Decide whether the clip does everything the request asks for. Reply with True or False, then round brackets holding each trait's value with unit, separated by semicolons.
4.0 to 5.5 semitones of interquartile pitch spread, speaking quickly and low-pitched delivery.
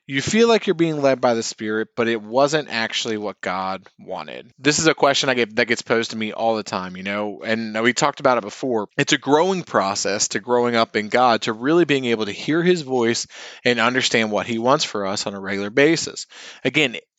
True (4.5 semitones; 235 wpm; 120 Hz)